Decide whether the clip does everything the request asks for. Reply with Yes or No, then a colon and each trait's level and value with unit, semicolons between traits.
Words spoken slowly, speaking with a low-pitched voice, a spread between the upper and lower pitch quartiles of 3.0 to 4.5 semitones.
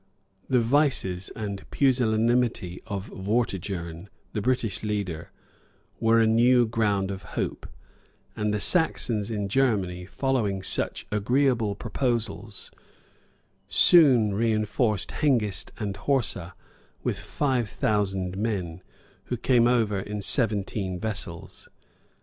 Yes: slow, 110 wpm; low, 105 Hz; average, 3.7 semitones